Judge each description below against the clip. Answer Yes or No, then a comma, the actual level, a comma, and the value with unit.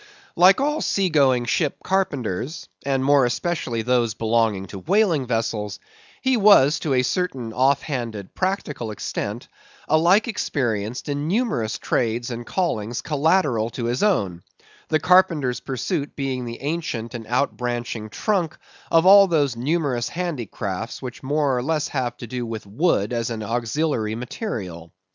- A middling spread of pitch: No, wide, 5.9 semitones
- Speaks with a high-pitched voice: No, low, 130 Hz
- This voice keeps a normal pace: Yes, average, 145 wpm